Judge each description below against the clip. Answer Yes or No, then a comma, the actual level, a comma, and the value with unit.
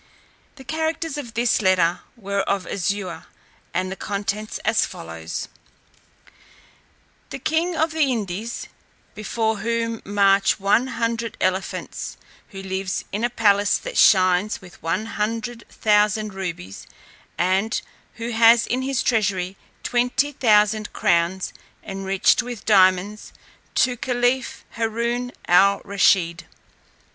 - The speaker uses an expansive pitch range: No, average, 3.7 semitones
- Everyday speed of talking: No, slow, 115 wpm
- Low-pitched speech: No, high, 210 Hz